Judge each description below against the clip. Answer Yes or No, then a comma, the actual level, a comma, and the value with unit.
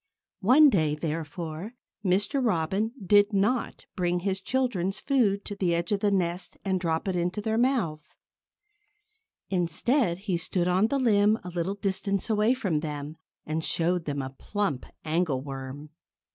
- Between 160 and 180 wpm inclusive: No, average, 150 wpm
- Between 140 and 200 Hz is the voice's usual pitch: Yes, medium, 185 Hz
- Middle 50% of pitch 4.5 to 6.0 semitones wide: No, average, 4.1 semitones